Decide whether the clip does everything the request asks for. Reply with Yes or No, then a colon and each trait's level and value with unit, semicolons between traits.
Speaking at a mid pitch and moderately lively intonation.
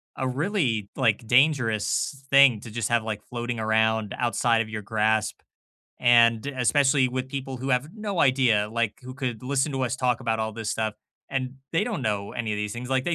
No: low, 120 Hz; average, 3.2 semitones